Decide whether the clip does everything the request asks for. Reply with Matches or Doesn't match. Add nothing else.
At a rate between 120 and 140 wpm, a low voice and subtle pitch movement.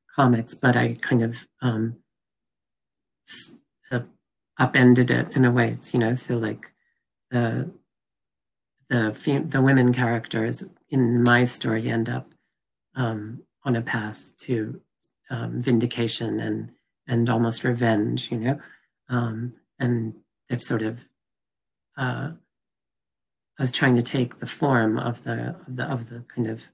Matches